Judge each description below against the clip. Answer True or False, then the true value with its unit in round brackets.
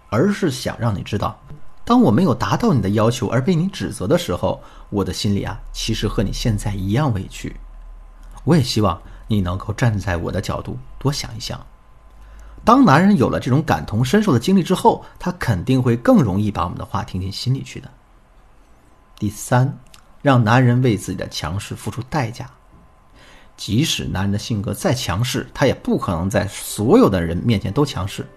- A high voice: False (110 Hz)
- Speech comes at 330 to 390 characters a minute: False (275 characters per minute)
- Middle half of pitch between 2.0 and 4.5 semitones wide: False (5.0 semitones)